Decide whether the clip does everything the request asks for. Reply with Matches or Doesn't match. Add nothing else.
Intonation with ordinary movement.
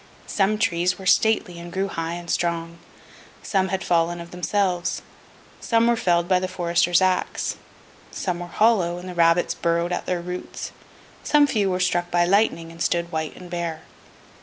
Doesn't match